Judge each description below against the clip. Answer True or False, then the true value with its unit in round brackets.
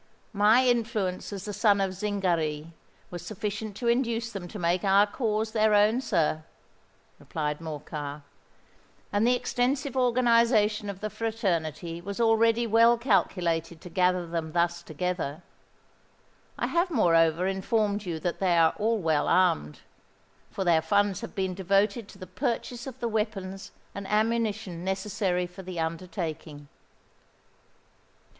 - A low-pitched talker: False (195 Hz)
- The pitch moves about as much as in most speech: True (4.5 semitones)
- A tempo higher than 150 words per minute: False (140 wpm)